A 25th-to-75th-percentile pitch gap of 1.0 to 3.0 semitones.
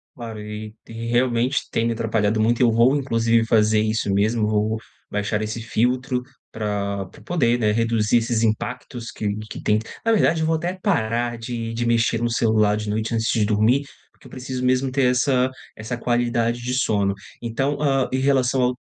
Yes: average, 2.7 semitones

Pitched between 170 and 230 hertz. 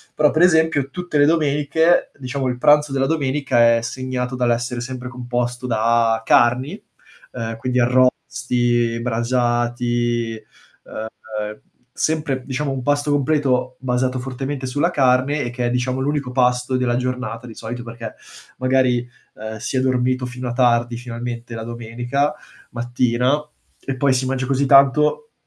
No: low, 125 Hz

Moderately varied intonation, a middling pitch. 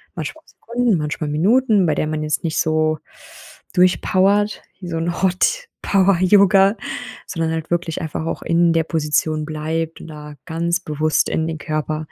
Yes: average, 3.2 semitones; medium, 165 Hz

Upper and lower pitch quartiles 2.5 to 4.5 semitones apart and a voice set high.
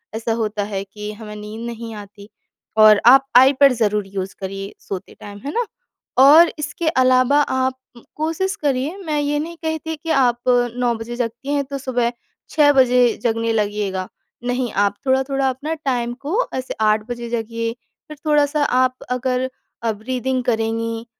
Yes: average, 4.1 semitones; very high, 250 Hz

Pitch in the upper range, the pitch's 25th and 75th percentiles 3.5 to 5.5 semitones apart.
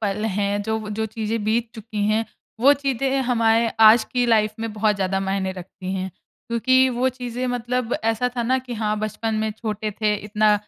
No: high, 220 Hz; narrow, 2.4 semitones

